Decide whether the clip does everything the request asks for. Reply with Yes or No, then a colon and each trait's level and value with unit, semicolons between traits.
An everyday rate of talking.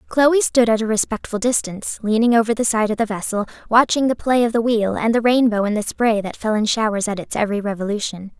No: fast, 235 wpm